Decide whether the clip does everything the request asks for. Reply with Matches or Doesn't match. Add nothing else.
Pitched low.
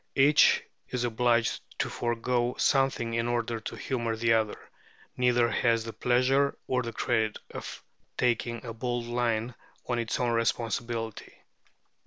Matches